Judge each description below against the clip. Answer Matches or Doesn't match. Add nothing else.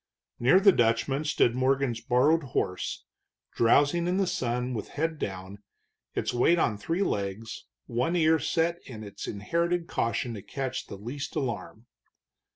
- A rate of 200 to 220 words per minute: Doesn't match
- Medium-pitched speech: Doesn't match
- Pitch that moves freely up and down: Matches